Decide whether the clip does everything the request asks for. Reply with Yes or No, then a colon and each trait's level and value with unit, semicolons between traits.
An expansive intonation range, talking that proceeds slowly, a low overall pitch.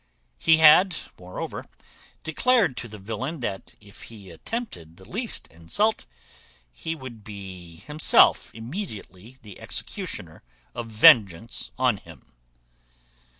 Yes: wide, 8.7 semitones; slow, 110 wpm; low, 115 Hz